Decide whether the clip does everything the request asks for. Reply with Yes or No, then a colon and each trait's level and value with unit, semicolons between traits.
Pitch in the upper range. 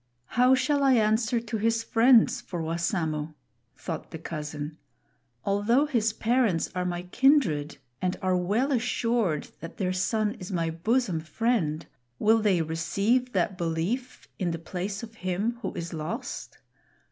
Yes: high, 200 Hz